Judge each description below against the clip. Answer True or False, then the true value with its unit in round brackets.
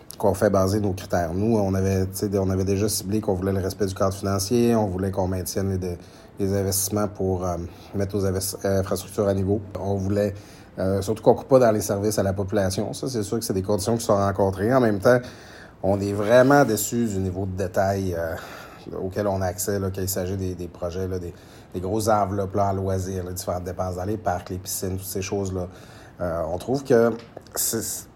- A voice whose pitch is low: True (100 Hz)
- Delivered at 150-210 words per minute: False (220 wpm)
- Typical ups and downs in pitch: False (2.1 semitones)